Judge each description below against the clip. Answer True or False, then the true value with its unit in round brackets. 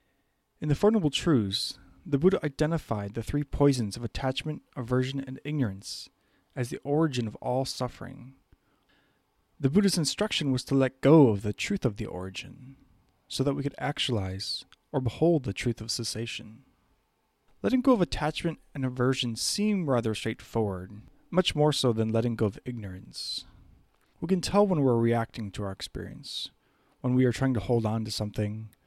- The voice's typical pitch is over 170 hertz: False (130 Hz)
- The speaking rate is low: False (170 wpm)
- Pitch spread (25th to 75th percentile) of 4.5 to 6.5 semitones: True (4.8 semitones)